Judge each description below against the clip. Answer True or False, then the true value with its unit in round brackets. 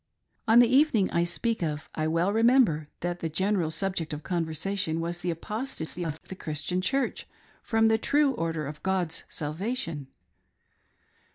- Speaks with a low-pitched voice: False (175 Hz)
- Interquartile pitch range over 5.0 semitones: True (5.6 semitones)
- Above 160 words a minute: False (155 wpm)